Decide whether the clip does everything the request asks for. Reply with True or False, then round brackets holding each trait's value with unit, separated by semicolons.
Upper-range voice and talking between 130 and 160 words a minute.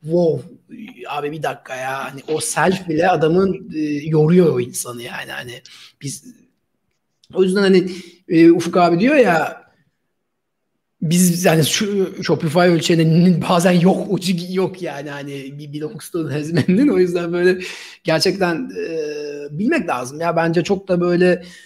False (170 Hz; 140 wpm)